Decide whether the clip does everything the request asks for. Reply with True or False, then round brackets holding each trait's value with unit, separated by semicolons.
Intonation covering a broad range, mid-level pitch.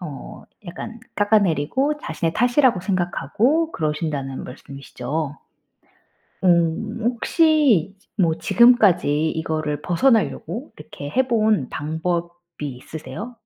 True (6.9 semitones; 175 Hz)